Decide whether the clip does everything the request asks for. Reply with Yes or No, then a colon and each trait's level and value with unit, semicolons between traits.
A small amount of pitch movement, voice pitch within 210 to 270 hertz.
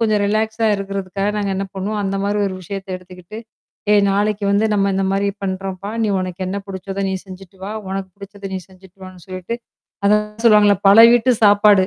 No: narrow, 1.6 semitones; high, 195 Hz